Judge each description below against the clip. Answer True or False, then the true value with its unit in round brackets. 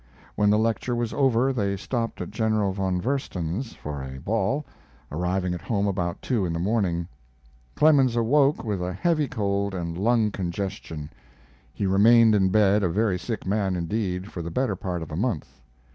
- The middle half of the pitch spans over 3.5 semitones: True (4.2 semitones)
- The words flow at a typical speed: True (175 wpm)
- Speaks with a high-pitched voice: False (100 Hz)